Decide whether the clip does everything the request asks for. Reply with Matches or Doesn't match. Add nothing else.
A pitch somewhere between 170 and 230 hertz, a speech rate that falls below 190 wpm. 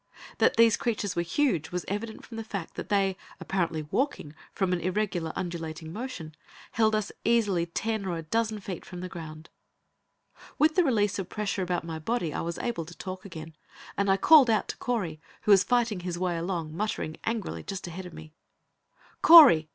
Doesn't match